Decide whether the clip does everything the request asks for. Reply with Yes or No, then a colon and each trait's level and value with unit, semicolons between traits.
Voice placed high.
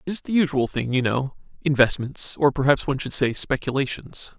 No: low, 135 Hz